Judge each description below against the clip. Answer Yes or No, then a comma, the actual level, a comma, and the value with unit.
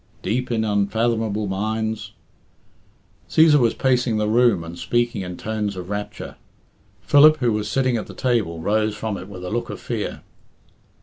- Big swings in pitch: No, average, 3.0 semitones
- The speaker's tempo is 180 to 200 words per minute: No, average, 170 wpm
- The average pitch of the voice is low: Yes, low, 110 Hz